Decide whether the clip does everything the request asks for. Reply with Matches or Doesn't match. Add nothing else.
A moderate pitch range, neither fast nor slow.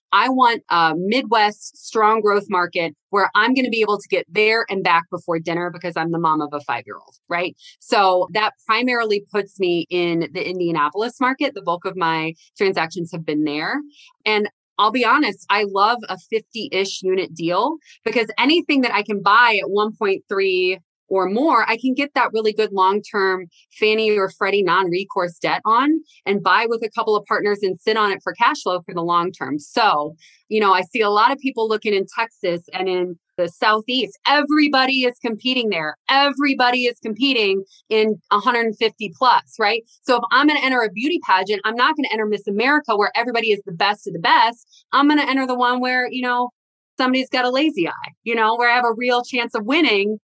Doesn't match